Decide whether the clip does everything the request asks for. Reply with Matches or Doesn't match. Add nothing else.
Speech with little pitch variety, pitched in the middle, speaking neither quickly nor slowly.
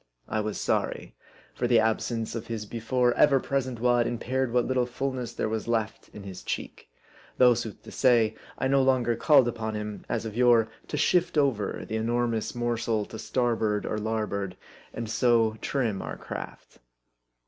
Doesn't match